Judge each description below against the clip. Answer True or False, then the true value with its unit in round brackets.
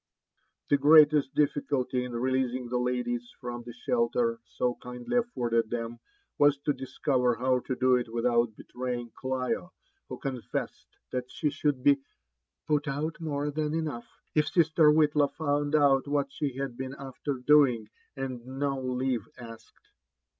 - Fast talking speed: False (155 wpm)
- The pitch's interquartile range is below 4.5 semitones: True (3.0 semitones)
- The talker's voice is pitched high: False (130 Hz)